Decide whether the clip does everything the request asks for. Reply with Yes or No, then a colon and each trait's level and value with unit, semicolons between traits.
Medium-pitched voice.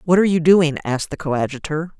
Yes: medium, 160 Hz